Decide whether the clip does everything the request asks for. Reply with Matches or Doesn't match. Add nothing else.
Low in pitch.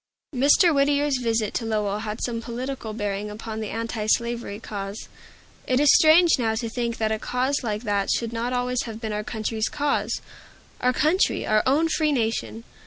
Doesn't match